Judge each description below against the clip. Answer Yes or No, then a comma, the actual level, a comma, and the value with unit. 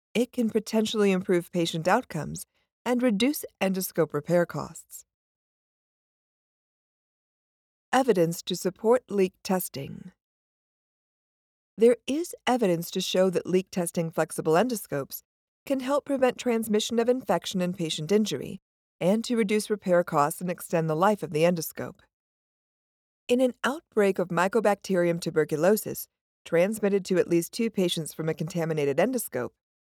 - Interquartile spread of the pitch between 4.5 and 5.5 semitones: Yes, average, 5.0 semitones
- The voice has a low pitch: No, high, 190 Hz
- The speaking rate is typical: No, slow, 130 wpm